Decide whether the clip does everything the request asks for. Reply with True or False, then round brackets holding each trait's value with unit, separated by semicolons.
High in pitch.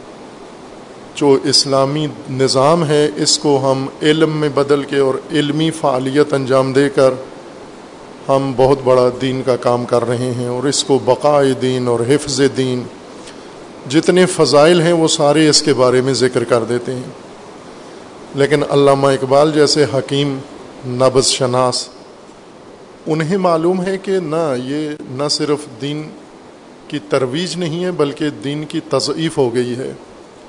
False (140 Hz)